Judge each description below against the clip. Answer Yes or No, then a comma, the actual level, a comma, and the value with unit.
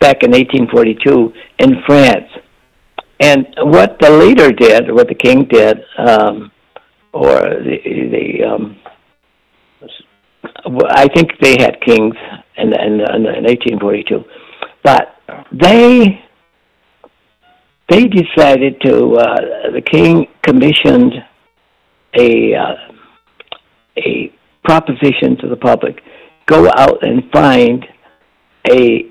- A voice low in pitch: No, medium, 145 Hz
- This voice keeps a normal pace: No, slow, 100 wpm